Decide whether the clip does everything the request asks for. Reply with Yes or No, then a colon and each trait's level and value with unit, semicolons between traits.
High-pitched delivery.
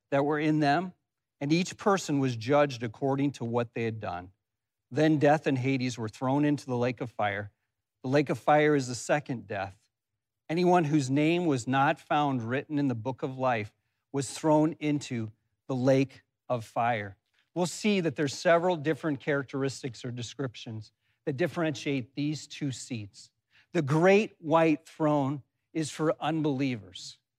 No: low, 135 Hz